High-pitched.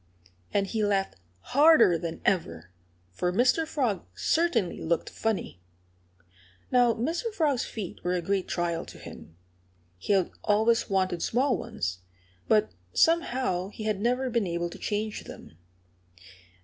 Yes: high, 205 Hz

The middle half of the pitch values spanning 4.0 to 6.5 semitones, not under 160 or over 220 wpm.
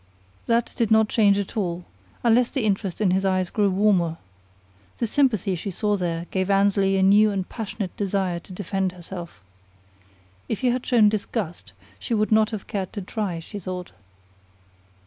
No: average, 2.7 semitones; average, 170 wpm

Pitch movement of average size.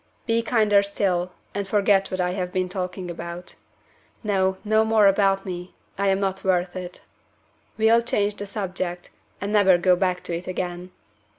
No: narrow, 2.1 semitones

